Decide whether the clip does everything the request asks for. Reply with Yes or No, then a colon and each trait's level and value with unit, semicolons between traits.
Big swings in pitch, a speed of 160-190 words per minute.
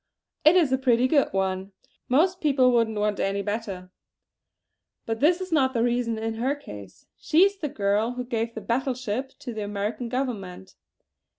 No: average, 4.3 semitones; average, 180 wpm